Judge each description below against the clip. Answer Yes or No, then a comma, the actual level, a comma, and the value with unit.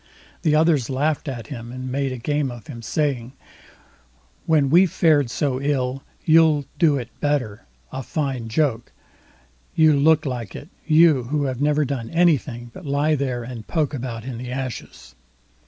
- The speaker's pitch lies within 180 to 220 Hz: No, medium, 140 Hz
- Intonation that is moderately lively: Yes, average, 3.7 semitones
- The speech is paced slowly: No, average, 155 wpm